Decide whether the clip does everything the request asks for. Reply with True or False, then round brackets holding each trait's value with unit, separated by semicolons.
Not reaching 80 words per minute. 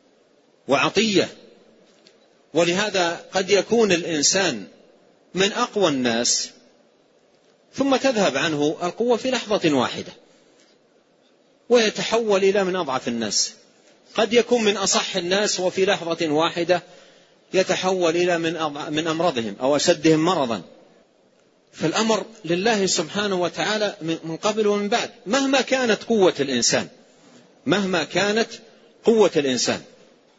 False (100 wpm)